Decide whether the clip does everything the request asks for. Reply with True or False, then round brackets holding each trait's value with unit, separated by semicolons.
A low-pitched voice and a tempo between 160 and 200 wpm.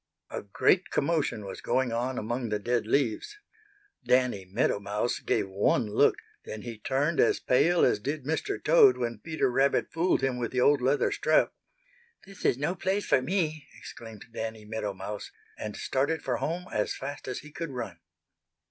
True (125 Hz; 175 wpm)